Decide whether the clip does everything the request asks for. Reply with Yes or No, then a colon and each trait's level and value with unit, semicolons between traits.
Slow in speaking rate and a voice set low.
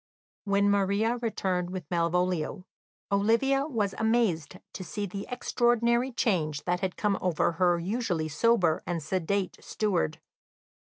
No: slow, 125 wpm; high, 195 Hz